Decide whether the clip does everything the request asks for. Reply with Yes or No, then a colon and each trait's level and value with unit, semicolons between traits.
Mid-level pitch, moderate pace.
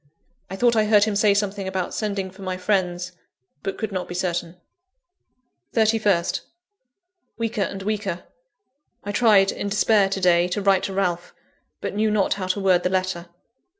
No: high, 195 Hz; average, 170 wpm